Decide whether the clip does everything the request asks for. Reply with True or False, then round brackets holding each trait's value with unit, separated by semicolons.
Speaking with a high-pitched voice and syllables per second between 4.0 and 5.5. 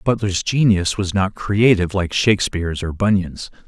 False (95 Hz; 4.9 syllables/s)